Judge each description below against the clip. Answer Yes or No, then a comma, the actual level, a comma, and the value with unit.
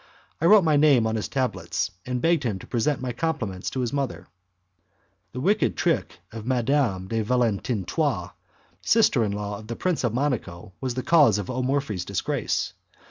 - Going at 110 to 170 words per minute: No, average, 185 wpm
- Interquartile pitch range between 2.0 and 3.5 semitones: No, average, 5.1 semitones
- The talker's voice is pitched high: No, low, 120 Hz